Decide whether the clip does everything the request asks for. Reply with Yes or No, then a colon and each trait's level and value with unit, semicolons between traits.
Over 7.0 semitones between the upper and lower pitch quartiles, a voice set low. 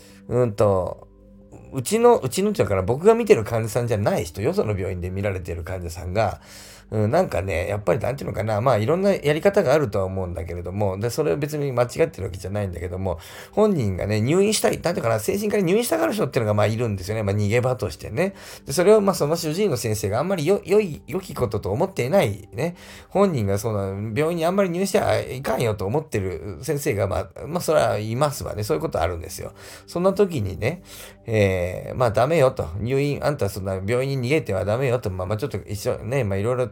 Yes: wide, 7.8 semitones; low, 115 Hz